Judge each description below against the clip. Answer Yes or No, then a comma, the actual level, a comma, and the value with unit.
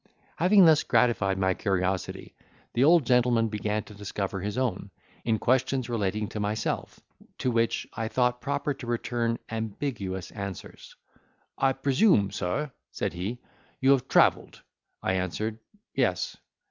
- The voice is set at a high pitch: No, low, 115 Hz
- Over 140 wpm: No, slow, 135 wpm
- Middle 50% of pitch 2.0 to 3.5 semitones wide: No, average, 4.5 semitones